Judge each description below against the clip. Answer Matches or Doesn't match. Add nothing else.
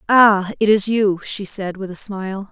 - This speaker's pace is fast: Matches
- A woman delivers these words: Matches